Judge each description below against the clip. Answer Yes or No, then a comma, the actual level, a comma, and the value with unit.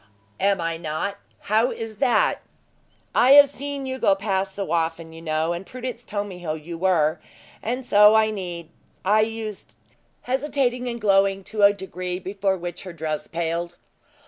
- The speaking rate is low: No, average, 170 wpm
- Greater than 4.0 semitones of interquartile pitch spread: Yes, average, 4.7 semitones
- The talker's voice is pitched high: Yes, high, 195 Hz